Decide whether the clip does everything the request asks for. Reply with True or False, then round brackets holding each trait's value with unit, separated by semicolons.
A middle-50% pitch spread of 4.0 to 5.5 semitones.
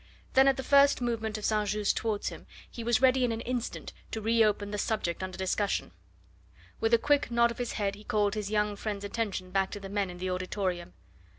False (3.0 semitones)